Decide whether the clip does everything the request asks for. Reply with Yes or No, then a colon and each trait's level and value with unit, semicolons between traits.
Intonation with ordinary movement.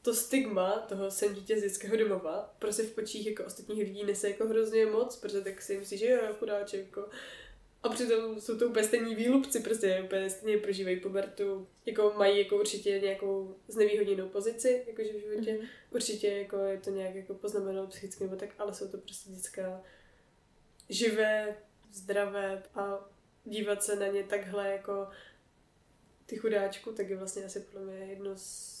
No: narrow, 1.9 semitones